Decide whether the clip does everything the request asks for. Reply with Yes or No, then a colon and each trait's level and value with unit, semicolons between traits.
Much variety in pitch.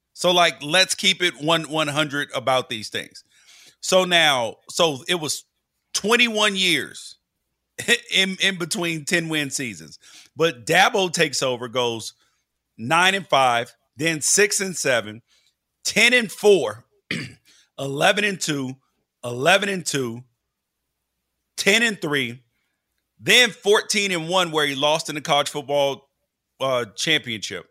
Yes: wide, 6.0 semitones